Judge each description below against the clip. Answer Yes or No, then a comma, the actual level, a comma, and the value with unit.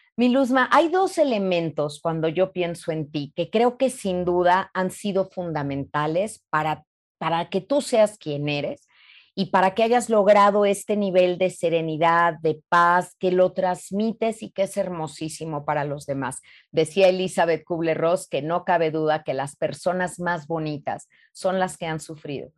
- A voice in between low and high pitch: Yes, medium, 175 Hz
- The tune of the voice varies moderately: Yes, average, 3.5 semitones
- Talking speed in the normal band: Yes, average, 165 wpm